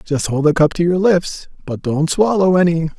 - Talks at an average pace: No, fast, 220 wpm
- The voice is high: No, medium, 165 Hz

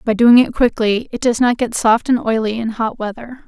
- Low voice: No, high, 230 Hz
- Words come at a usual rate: No, fast, 240 wpm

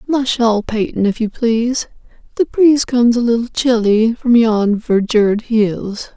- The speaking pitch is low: No, high, 230 Hz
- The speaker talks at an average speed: Yes, average, 145 wpm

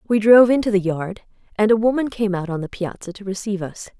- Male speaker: No, female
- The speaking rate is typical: No, fast, 240 wpm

